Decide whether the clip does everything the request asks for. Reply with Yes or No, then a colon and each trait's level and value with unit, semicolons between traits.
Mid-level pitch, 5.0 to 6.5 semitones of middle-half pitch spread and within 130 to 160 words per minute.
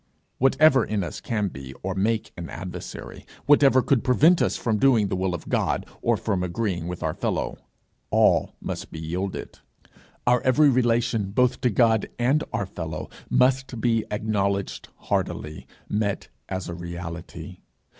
No: low, 105 Hz; wide, 5.6 semitones; average, 155 wpm